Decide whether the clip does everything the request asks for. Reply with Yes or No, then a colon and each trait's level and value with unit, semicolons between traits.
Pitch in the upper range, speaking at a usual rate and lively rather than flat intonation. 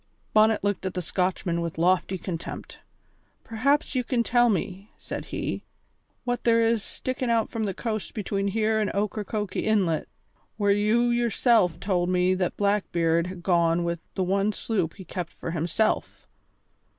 No: high, 200 Hz; average, 160 wpm; average, 3.8 semitones